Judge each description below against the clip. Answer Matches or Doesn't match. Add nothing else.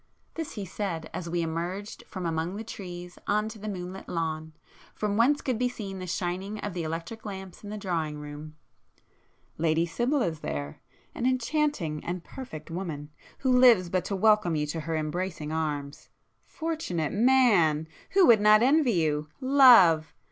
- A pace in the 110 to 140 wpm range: Doesn't match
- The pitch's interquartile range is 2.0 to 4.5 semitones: Doesn't match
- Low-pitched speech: Doesn't match